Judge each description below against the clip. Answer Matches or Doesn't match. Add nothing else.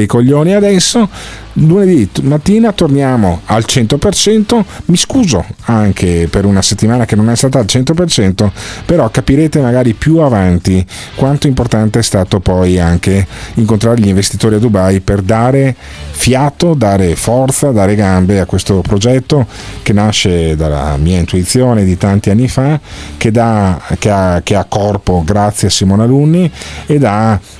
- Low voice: Matches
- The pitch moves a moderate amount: Doesn't match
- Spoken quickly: Doesn't match